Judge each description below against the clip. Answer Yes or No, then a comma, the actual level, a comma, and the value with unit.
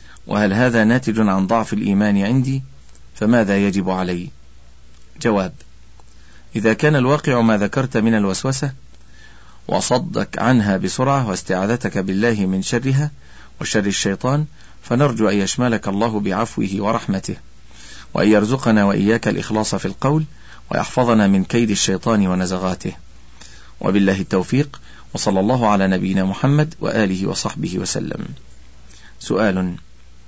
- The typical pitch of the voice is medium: No, low, 100 Hz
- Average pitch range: Yes, average, 4.8 semitones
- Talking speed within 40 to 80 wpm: No, average, 110 wpm